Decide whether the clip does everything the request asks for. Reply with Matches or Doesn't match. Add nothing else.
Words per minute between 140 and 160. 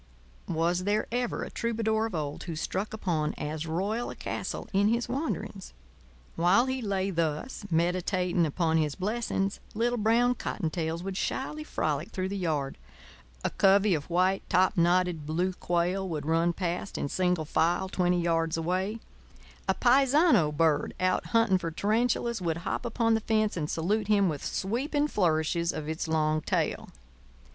Matches